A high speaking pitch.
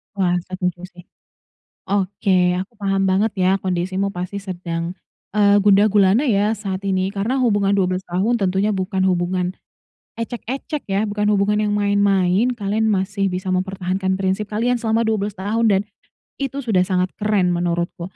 Yes: high, 195 Hz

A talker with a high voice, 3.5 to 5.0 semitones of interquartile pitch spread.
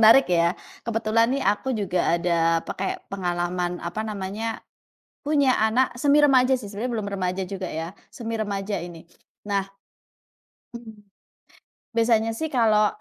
Yes: high, 215 Hz; average, 4.2 semitones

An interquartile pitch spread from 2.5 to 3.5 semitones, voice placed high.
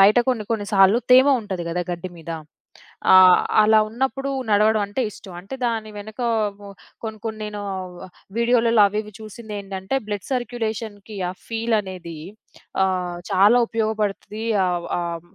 Yes: average, 2.8 semitones; high, 210 Hz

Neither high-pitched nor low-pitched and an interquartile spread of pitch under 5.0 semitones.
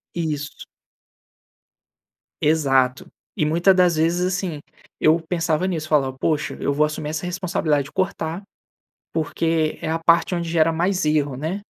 Yes: medium, 160 Hz; narrow, 2.5 semitones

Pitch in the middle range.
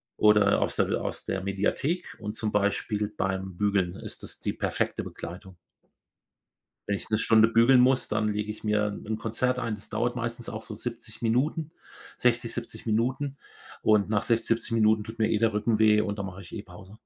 No: low, 110 Hz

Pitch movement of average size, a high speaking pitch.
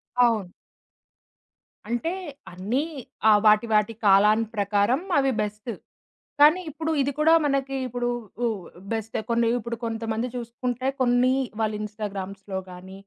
Yes: average, 3.2 semitones; high, 225 Hz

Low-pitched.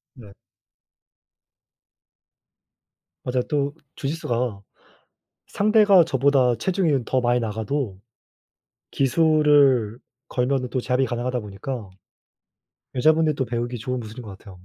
Yes: low, 125 Hz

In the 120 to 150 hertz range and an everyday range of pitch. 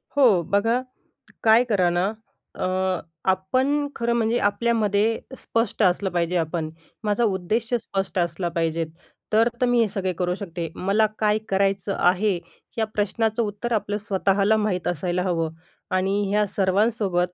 No: high, 200 Hz; average, 3.5 semitones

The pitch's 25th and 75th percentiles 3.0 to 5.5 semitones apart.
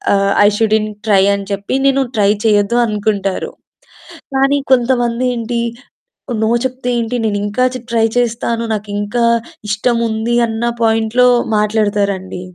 No: narrow, 2.6 semitones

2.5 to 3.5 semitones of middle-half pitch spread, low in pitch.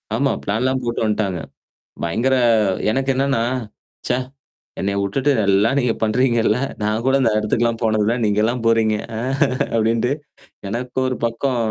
Yes: average, 2.9 semitones; low, 115 Hz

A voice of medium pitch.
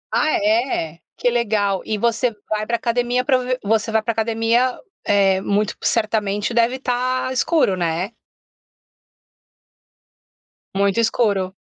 No: high, 225 Hz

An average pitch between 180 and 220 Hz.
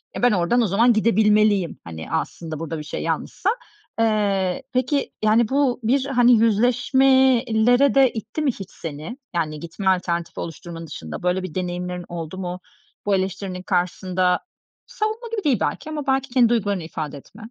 Yes: high, 205 Hz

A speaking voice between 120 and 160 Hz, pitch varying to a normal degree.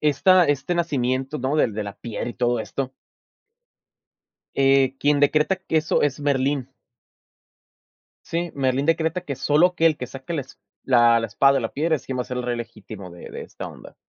Yes: low, 135 Hz; average, 3.6 semitones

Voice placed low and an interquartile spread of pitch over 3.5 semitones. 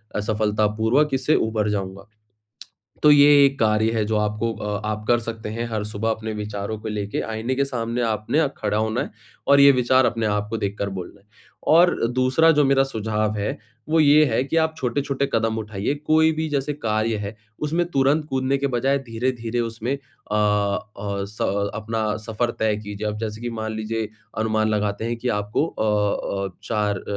Yes: low, 110 Hz; average, 3.9 semitones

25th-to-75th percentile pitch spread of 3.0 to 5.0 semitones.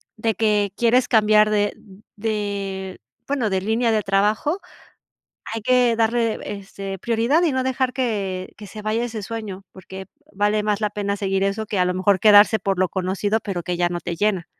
No: narrow, 2.6 semitones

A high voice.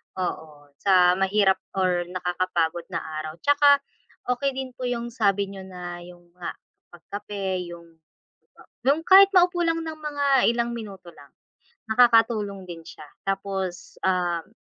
Yes: high, 195 Hz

